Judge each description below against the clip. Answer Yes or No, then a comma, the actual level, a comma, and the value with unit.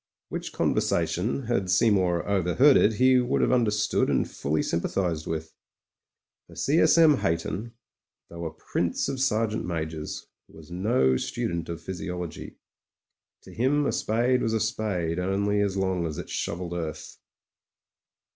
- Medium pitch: No, very low, 95 Hz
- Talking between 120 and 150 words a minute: Yes, average, 145 wpm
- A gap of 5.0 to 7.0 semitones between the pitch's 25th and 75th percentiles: Yes, average, 5.3 semitones